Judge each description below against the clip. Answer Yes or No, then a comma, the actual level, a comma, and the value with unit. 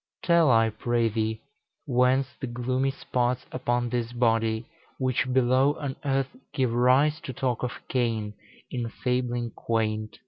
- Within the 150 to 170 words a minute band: No, average, 140 wpm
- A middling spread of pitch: No, narrow, 2.1 semitones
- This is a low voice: Yes, low, 125 Hz